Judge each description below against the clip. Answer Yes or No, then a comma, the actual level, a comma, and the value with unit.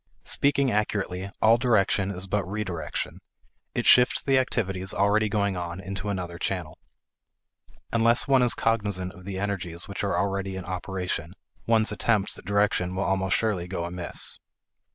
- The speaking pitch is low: Yes, low, 100 Hz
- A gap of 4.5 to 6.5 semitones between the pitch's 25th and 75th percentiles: No, average, 2.7 semitones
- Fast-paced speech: No, average, 155 wpm